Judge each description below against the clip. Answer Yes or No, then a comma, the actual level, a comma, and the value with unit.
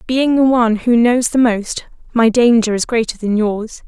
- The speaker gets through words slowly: No, average, 200 wpm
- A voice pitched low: No, high, 230 Hz